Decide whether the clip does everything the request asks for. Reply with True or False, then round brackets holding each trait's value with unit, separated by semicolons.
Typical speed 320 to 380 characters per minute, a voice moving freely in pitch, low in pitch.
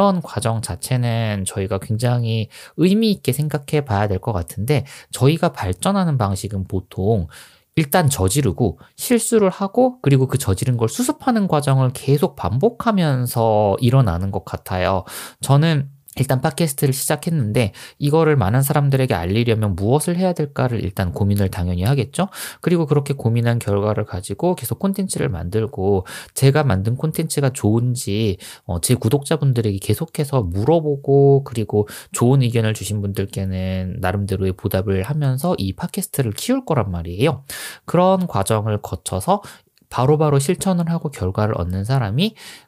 True (345 characters per minute; 7.1 semitones; 125 Hz)